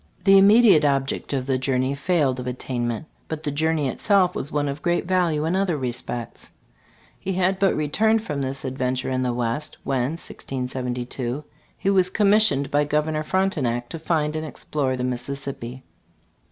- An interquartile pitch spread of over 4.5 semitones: Yes, average, 5.1 semitones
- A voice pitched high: No, medium, 145 Hz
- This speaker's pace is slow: No, average, 165 wpm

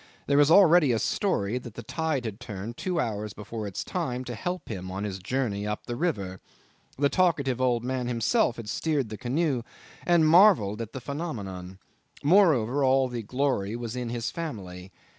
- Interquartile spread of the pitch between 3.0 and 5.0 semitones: No, wide, 5.6 semitones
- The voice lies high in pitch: No, low, 125 Hz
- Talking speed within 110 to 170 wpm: No, average, 185 wpm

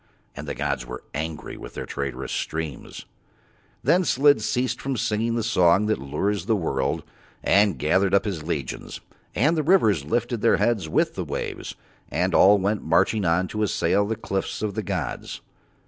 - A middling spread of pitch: No, wide, 6.0 semitones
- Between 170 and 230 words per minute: Yes, average, 180 wpm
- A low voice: Yes, low, 100 Hz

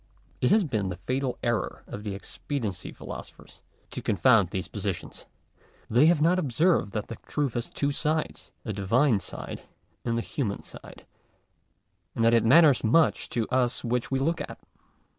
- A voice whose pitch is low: Yes, low, 125 Hz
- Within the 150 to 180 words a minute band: Yes, average, 165 wpm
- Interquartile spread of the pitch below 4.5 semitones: No, average, 4.9 semitones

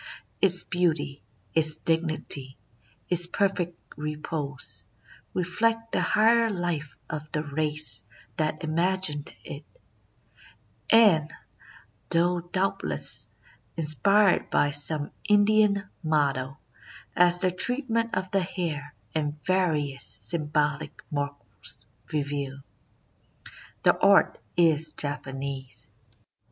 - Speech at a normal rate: No, slow, 90 wpm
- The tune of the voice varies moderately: Yes, average, 4.1 semitones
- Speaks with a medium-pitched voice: Yes, medium, 155 Hz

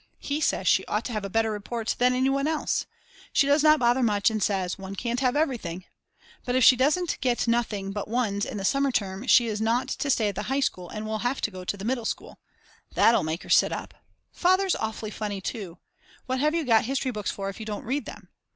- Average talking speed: No, fast, 245 wpm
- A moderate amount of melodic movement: Yes, average, 4.3 semitones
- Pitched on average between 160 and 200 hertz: No, high, 230 Hz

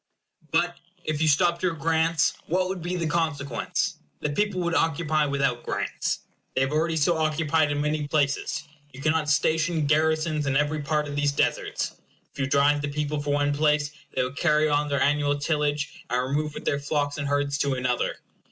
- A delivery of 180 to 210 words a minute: Yes, average, 190 wpm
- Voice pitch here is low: No, medium, 150 Hz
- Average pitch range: No, narrow, 1.8 semitones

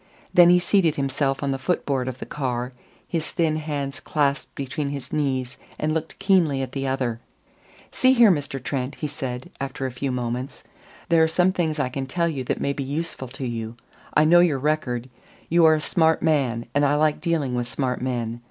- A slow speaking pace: No, fast, 205 wpm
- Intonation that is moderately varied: Yes, average, 3.6 semitones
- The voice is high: No, medium, 140 Hz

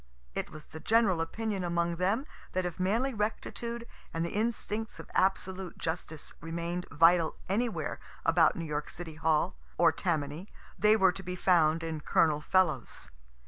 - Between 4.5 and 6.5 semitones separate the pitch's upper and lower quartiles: No, average, 4.0 semitones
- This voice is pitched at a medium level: Yes, medium, 180 Hz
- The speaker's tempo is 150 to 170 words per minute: Yes, average, 155 wpm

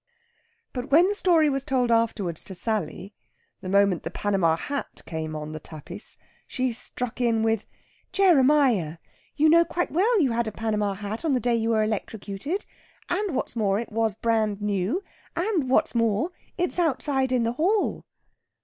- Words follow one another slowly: No, average, 170 wpm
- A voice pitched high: Yes, high, 230 Hz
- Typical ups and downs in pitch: No, wide, 6.2 semitones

